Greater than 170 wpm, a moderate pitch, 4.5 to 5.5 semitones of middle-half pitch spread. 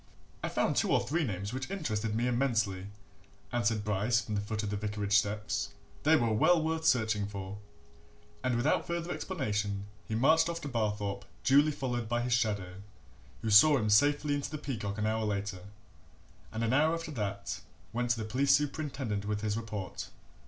No: average, 180 wpm; low, 110 Hz; average, 5.1 semitones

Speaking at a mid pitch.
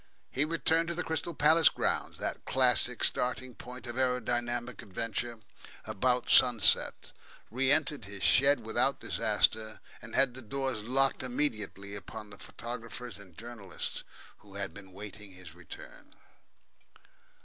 No: low, 120 Hz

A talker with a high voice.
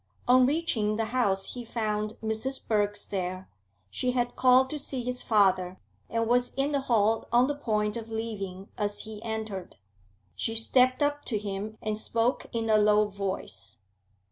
Yes: high, 220 Hz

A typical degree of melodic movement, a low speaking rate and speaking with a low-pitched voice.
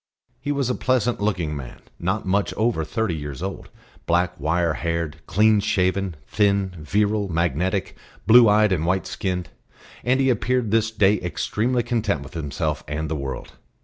No: average, 4.7 semitones; average, 160 wpm; very low, 95 Hz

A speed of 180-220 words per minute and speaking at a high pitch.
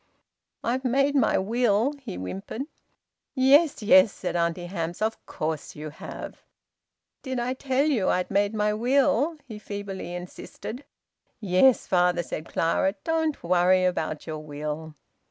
No: slow, 135 wpm; high, 205 Hz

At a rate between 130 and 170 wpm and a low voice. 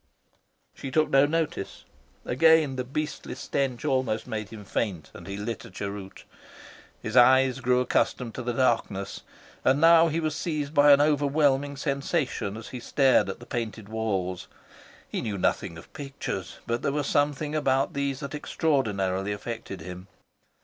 Yes: average, 160 wpm; low, 130 Hz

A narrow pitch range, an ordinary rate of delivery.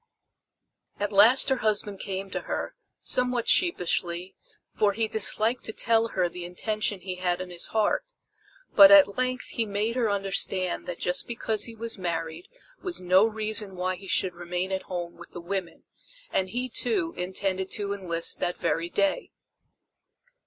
No: average, 3.8 semitones; average, 165 wpm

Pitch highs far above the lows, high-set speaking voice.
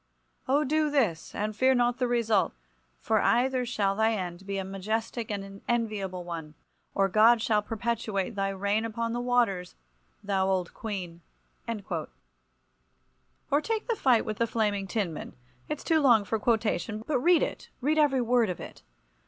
No: average, 3.8 semitones; high, 220 Hz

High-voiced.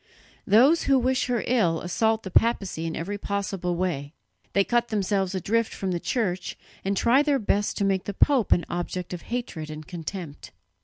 Yes: high, 195 Hz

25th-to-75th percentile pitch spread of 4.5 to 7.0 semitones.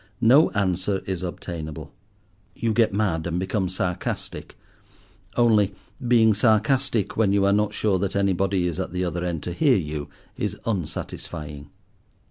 No: average, 3.5 semitones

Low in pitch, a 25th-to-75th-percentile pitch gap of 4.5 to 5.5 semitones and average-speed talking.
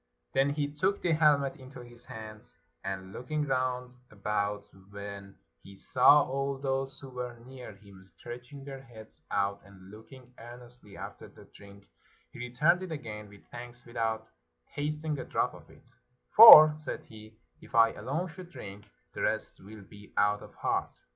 Yes: low, 120 Hz; average, 5.0 semitones; average, 175 wpm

